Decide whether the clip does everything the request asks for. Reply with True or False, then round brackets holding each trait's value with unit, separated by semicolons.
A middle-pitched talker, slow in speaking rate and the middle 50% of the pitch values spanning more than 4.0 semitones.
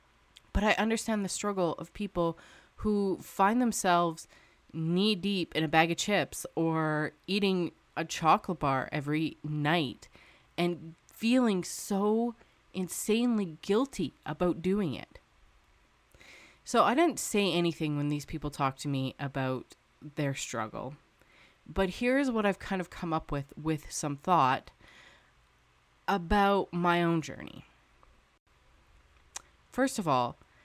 True (170 Hz; 130 wpm; 5.1 semitones)